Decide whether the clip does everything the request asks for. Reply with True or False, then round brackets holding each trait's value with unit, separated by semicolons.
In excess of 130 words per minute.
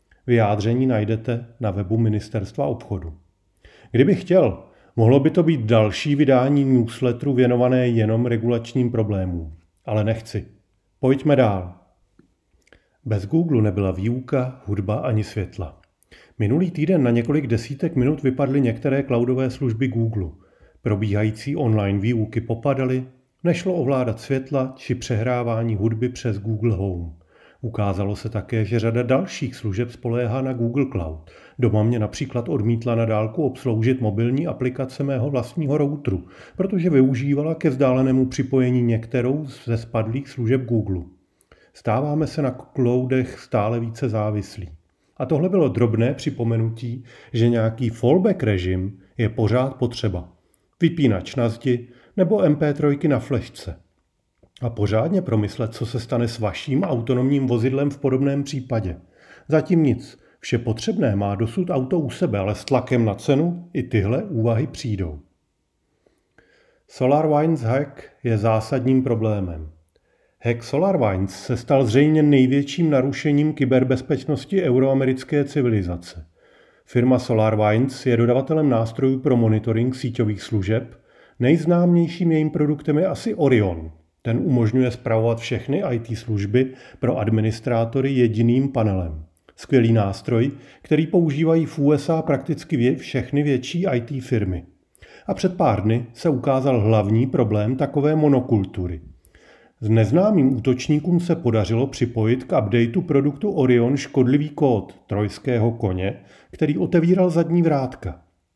False (125 wpm)